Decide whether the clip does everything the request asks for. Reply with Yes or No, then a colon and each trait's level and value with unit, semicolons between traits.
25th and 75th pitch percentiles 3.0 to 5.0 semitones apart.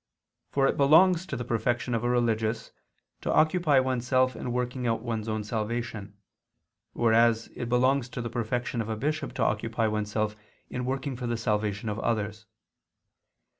No: narrow, 2.6 semitones